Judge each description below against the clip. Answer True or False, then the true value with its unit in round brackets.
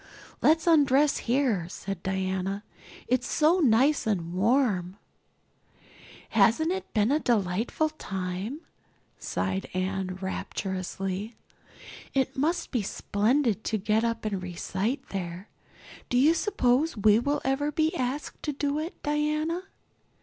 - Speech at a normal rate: False (120 wpm)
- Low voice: False (230 Hz)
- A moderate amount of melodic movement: False (7.2 semitones)